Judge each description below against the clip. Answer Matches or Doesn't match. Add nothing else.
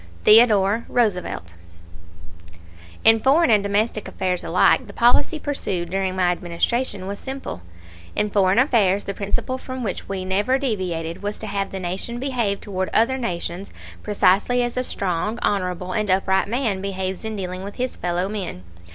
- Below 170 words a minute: Matches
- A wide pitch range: Doesn't match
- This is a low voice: Doesn't match